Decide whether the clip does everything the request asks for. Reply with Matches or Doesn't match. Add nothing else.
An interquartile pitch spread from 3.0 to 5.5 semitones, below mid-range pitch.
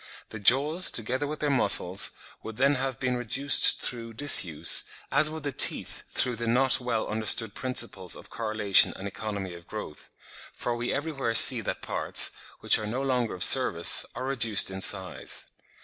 Matches